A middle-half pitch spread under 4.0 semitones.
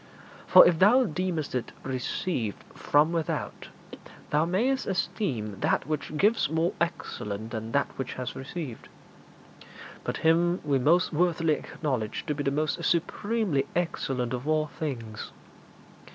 No: average, 5.0 semitones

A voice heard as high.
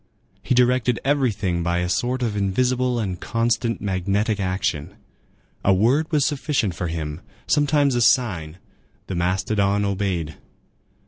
No: low, 105 Hz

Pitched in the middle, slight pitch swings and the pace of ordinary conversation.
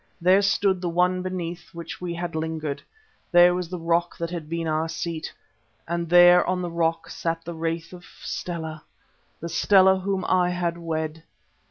Yes: medium, 170 Hz; narrow, 1.5 semitones; average, 175 wpm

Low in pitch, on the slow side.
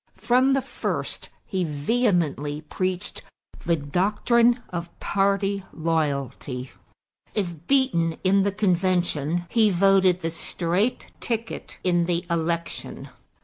No: medium, 180 Hz; slow, 105 wpm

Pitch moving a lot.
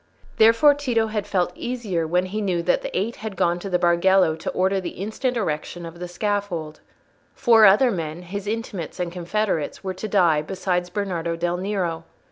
No: average, 3.6 semitones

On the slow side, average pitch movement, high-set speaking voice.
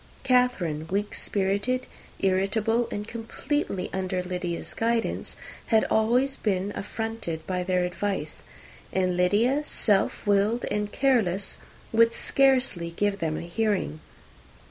Yes: slow, 115 wpm; average, 4.0 semitones; high, 205 Hz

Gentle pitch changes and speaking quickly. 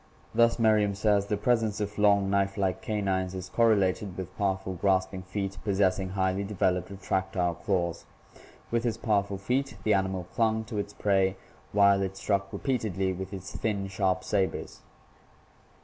No: narrow, 1.8 semitones; average, 150 wpm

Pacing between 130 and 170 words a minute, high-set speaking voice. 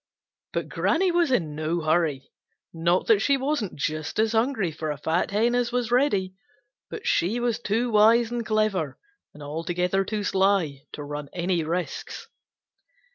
Yes: average, 160 wpm; high, 195 Hz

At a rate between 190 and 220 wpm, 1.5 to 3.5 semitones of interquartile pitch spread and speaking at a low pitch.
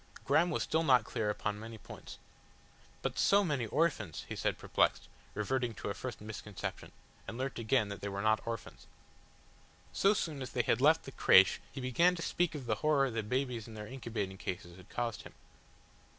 No: average, 195 wpm; average, 4.6 semitones; low, 120 Hz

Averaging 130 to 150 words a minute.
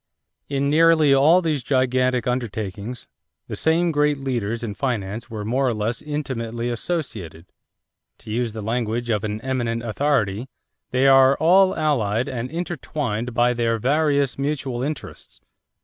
Yes: average, 140 wpm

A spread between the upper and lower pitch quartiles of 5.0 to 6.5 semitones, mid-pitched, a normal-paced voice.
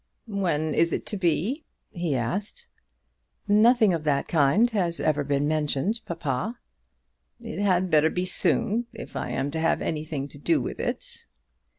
Yes: wide, 5.6 semitones; medium, 170 Hz; average, 160 wpm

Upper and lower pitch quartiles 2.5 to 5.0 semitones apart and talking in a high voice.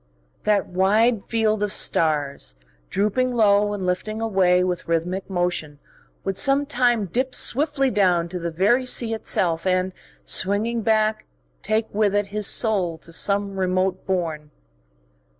Yes: average, 3.4 semitones; high, 200 Hz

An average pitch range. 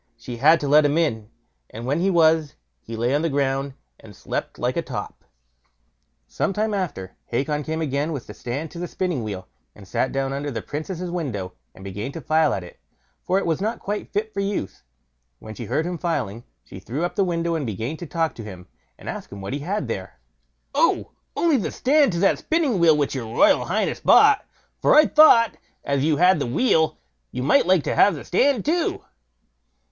No: wide, 7.1 semitones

